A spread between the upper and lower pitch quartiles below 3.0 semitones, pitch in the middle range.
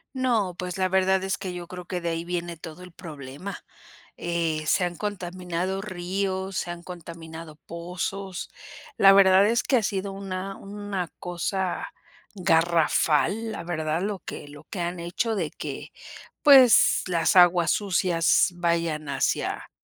Yes: narrow, 2.4 semitones; medium, 180 Hz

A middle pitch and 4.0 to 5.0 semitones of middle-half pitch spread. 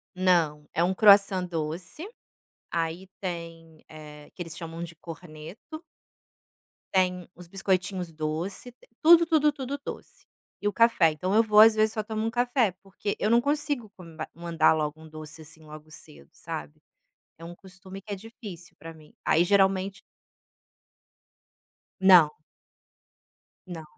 Yes: medium, 180 Hz; average, 4.5 semitones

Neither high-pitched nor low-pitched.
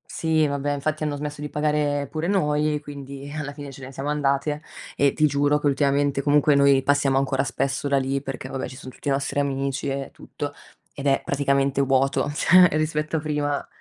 Yes: medium, 145 Hz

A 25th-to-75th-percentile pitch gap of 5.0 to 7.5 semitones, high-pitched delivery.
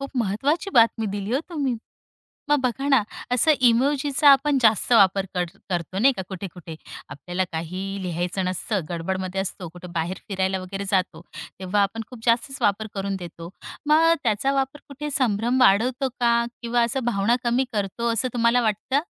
Yes: wide, 5.4 semitones; high, 220 Hz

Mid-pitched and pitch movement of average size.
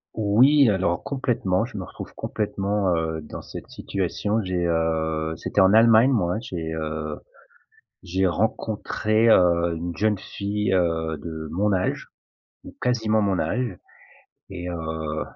No: very low, 95 Hz; average, 4.7 semitones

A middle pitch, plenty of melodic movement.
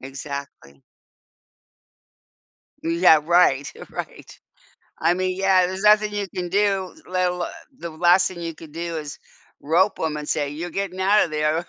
No: medium, 175 Hz; average, 3.4 semitones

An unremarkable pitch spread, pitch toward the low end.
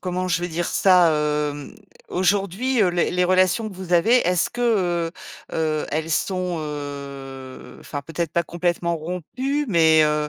No: average, 3.3 semitones; medium, 170 Hz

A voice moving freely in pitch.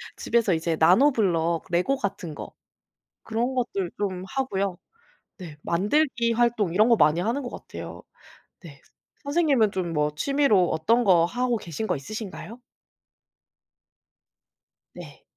Yes: wide, 5.9 semitones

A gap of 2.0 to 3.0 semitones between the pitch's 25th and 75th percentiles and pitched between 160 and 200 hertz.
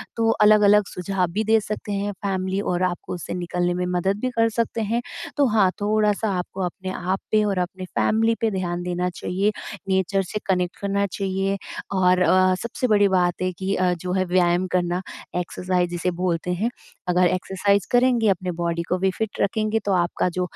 Yes: narrow, 2.5 semitones; high, 190 Hz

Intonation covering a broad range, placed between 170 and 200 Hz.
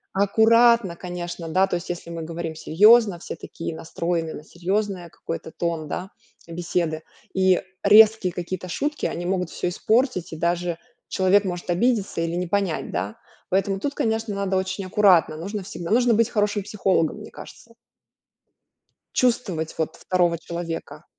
No: average, 3.5 semitones; medium, 185 Hz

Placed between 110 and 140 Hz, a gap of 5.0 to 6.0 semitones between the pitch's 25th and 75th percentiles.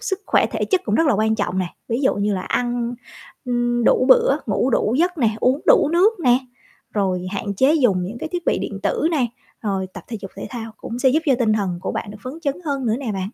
No: high, 240 Hz; wide, 5.5 semitones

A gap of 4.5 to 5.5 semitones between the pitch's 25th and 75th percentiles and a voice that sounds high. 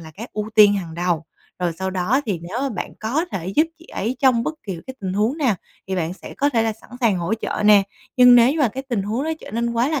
Yes: average, 4.8 semitones; high, 220 Hz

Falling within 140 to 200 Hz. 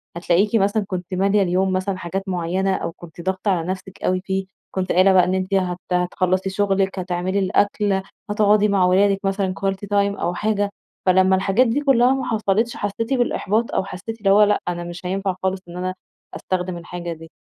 Yes: high, 190 Hz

